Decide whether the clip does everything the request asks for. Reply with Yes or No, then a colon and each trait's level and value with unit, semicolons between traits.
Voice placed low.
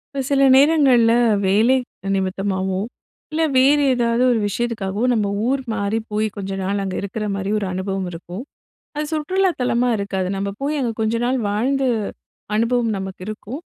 No: high, 220 Hz